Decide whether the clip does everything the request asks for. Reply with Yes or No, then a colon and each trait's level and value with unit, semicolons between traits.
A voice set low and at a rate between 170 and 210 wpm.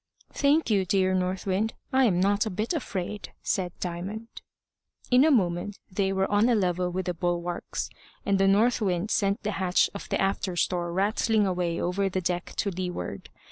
No: high, 195 Hz; average, 180 wpm